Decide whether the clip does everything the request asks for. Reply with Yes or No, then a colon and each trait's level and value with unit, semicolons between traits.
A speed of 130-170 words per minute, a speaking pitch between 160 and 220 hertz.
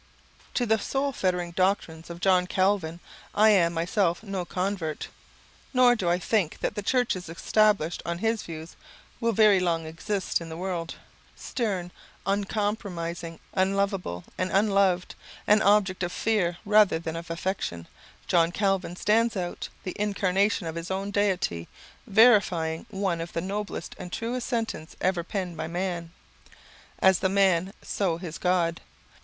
Yes: average, 150 wpm; medium, 185 Hz